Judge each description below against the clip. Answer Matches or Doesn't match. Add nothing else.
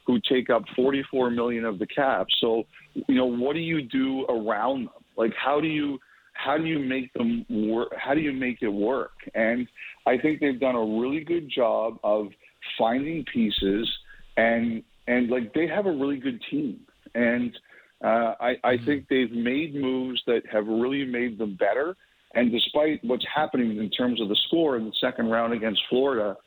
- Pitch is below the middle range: Matches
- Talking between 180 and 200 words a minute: Matches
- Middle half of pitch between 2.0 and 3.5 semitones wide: Doesn't match